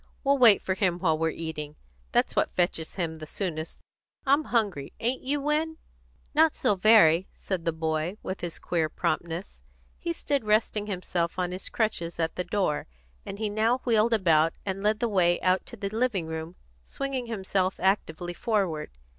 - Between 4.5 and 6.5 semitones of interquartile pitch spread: Yes, average, 4.9 semitones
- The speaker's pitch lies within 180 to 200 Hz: Yes, high, 190 Hz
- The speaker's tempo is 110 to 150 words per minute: No, average, 175 wpm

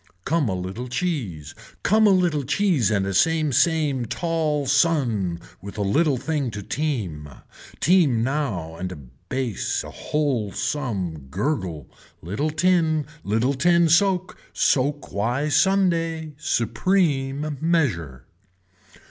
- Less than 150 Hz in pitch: Yes, medium, 140 Hz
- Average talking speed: No, slow, 120 wpm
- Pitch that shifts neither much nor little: No, wide, 7.9 semitones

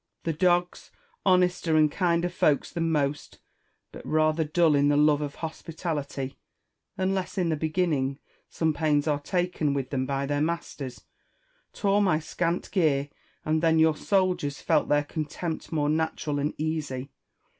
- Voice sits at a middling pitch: Yes, medium, 155 Hz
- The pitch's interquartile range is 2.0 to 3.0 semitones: Yes, average, 2.7 semitones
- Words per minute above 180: No, average, 150 wpm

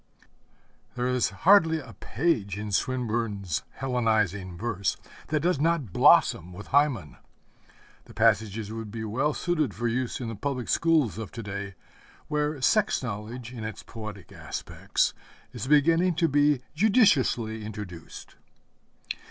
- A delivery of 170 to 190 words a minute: No, slow, 135 wpm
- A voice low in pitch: Yes, low, 120 Hz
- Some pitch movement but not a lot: No, wide, 6.0 semitones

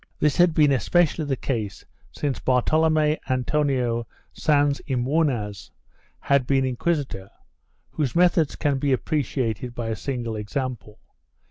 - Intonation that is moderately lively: Yes, average, 3.9 semitones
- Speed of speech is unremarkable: No, slow, 130 wpm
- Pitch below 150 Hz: Yes, low, 135 Hz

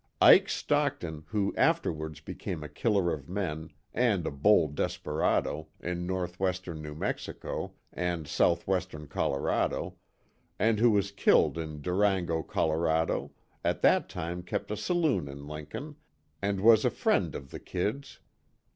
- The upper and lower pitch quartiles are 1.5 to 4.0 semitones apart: No, average, 4.5 semitones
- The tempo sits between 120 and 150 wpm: Yes, slow, 135 wpm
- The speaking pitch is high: No, very low, 90 Hz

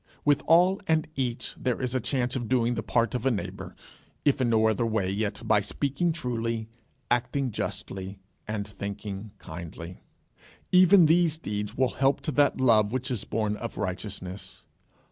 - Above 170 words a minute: No, average, 165 wpm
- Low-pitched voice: Yes, low, 115 Hz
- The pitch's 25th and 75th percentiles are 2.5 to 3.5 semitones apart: No, average, 4.5 semitones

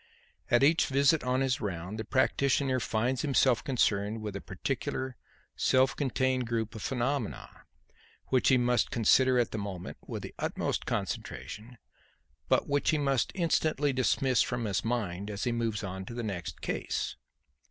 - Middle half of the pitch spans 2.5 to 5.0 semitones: Yes, average, 3.8 semitones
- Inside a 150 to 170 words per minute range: Yes, average, 160 wpm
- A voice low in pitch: Yes, low, 125 Hz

